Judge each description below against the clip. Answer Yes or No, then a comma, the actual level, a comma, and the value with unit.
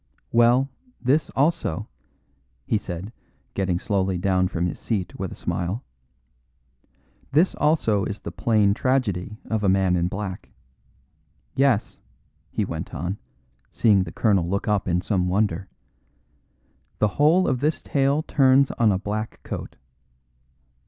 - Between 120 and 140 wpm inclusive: Yes, slow, 135 wpm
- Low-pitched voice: Yes, low, 105 Hz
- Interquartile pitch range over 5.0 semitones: Yes, wide, 5.5 semitones